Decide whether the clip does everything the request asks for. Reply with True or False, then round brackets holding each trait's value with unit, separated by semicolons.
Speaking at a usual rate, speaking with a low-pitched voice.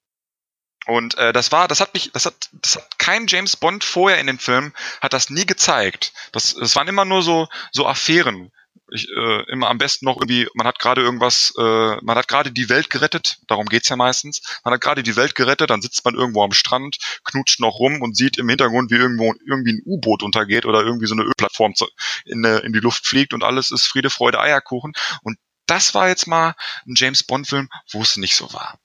False (225 wpm; 130 Hz)